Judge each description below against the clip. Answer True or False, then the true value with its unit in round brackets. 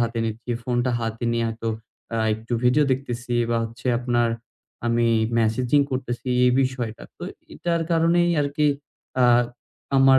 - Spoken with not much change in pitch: True (2.3 semitones)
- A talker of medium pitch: False (120 Hz)